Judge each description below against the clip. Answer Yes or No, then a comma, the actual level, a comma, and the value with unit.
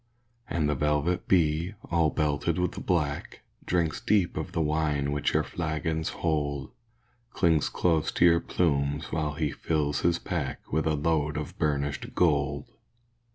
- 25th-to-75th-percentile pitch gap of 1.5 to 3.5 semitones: Yes, narrow, 2.4 semitones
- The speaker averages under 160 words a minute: Yes, average, 150 wpm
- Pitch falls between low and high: No, very low, 75 Hz